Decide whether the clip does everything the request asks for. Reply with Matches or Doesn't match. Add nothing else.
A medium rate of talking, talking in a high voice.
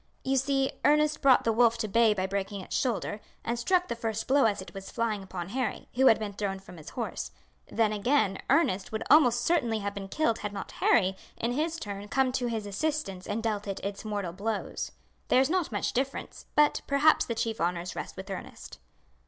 Doesn't match